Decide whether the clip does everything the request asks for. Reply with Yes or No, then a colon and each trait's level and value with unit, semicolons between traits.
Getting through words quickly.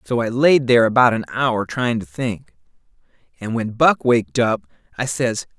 No: average, 185 wpm